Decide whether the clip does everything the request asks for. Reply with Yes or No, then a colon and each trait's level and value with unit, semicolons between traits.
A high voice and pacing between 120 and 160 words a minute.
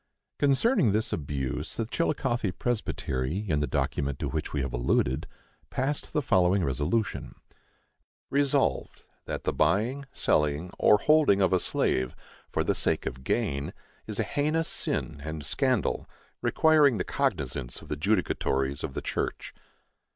No: very low, 90 Hz; average, 145 wpm